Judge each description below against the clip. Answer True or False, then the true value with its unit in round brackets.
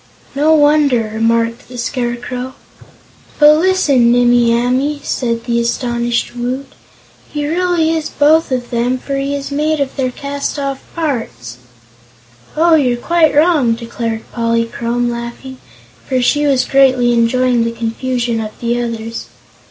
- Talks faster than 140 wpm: False (135 wpm)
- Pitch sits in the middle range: False (250 Hz)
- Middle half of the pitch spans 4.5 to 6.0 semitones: False (3.3 semitones)